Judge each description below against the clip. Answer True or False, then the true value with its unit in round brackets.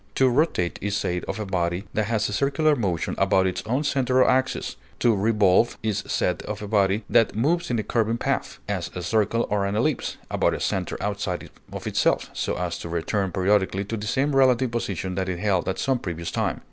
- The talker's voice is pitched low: True (105 Hz)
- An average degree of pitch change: True (4.1 semitones)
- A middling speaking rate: False (215 wpm)